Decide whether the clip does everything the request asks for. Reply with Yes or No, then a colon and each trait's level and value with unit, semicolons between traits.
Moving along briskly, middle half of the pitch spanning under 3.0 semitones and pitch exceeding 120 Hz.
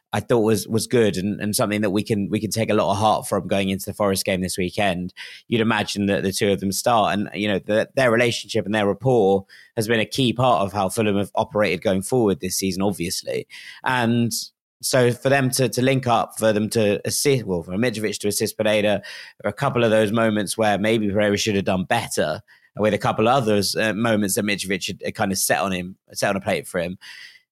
No: fast, 240 wpm; narrow, 2.6 semitones; low, 105 Hz